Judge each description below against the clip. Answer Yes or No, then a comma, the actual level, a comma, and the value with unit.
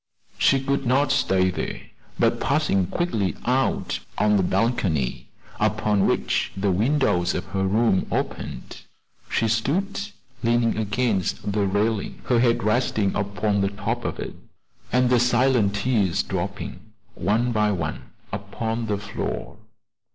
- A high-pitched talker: No, low, 105 Hz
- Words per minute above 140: No, slow, 135 wpm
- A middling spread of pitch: Yes, average, 3.7 semitones